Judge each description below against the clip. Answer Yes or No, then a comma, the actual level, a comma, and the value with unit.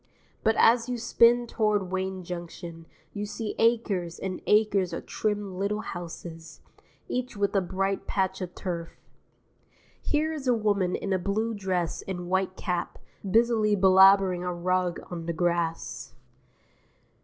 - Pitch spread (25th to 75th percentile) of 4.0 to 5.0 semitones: No, average, 3.2 semitones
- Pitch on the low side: No, high, 190 Hz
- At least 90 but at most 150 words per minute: Yes, average, 145 wpm